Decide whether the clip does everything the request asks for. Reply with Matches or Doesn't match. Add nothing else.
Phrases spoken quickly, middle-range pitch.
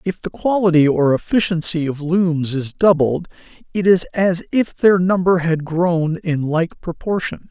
Doesn't match